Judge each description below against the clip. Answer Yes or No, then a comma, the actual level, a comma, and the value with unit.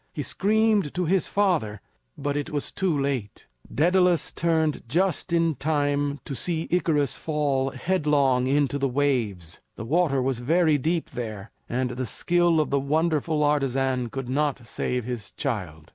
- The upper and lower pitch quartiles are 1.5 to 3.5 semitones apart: No, average, 4.2 semitones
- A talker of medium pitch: Yes, medium, 145 Hz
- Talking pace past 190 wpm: No, average, 155 wpm